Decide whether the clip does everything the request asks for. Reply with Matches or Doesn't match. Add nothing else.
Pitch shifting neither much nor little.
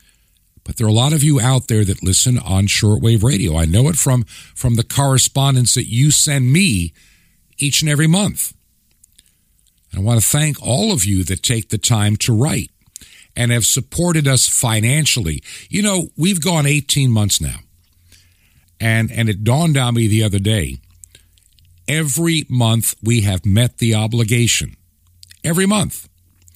Doesn't match